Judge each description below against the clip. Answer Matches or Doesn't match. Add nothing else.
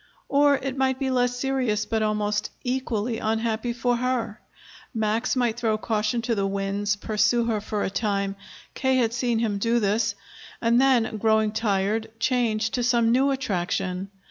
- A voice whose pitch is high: Matches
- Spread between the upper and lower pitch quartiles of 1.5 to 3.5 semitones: Matches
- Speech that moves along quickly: Doesn't match